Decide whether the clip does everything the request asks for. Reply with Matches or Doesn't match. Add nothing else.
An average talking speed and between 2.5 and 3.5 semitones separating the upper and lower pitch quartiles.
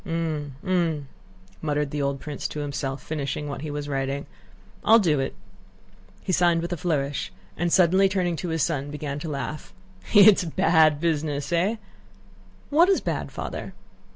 Matches